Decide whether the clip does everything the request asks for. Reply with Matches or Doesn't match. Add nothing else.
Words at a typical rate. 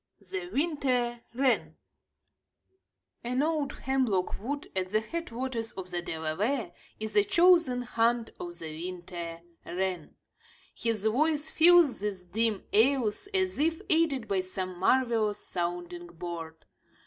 Doesn't match